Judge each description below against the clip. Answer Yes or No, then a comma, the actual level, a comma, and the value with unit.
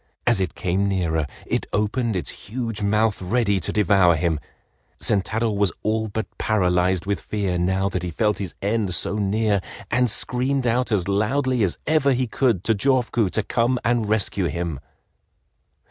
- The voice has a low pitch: Yes, low, 105 Hz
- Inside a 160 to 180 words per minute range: Yes, average, 165 wpm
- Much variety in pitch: No, average, 3.6 semitones